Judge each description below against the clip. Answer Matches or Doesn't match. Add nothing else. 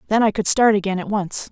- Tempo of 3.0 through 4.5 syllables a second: Doesn't match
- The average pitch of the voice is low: Doesn't match